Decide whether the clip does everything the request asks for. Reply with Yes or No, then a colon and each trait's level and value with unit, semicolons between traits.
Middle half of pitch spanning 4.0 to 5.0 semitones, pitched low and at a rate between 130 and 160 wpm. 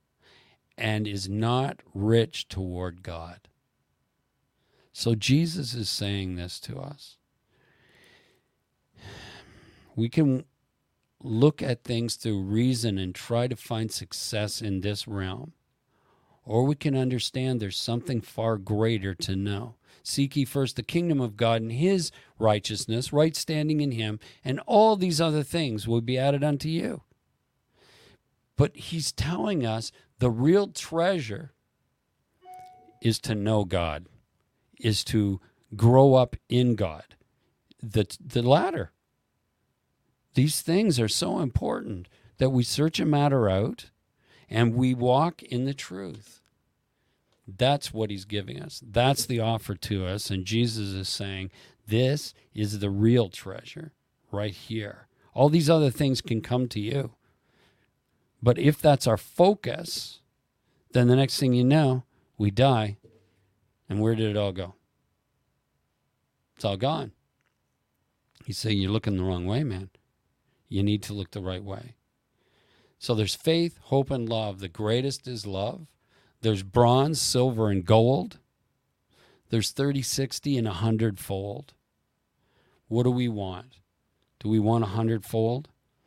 Yes: average, 4.5 semitones; low, 115 Hz; slow, 135 wpm